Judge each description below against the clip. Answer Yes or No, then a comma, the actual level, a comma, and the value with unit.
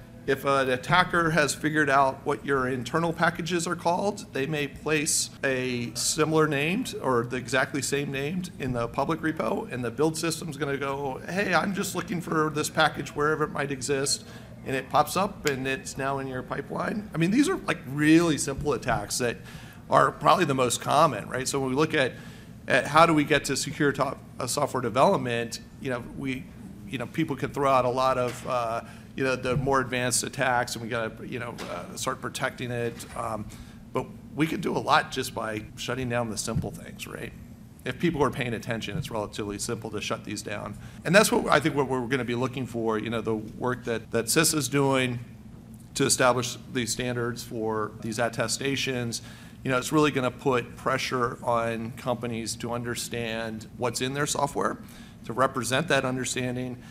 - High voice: No, low, 130 Hz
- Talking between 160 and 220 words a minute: Yes, average, 200 wpm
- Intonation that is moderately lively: Yes, average, 4.0 semitones